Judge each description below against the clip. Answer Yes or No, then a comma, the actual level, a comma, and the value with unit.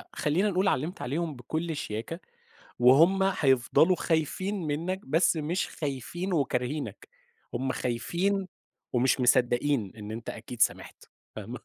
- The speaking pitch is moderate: Yes, medium, 150 Hz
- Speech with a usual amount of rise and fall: No, wide, 5.8 semitones